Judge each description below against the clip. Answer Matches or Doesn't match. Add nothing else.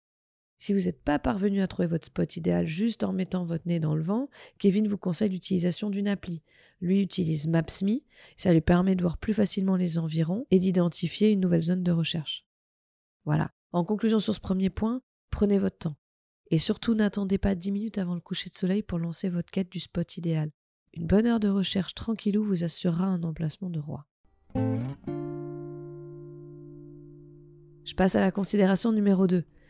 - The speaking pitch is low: Doesn't match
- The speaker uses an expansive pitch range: Doesn't match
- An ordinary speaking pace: Matches